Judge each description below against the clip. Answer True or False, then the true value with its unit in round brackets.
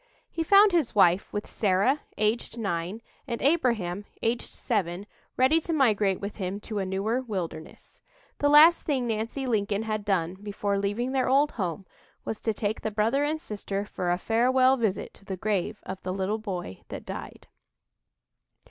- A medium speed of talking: True (170 wpm)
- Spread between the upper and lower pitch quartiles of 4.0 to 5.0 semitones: True (4.6 semitones)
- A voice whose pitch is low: False (215 Hz)